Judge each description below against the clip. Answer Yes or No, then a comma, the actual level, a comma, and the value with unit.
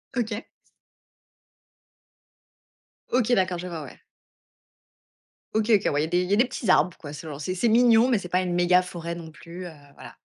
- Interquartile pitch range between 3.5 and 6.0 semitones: Yes, average, 4.4 semitones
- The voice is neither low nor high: Yes, medium, 180 Hz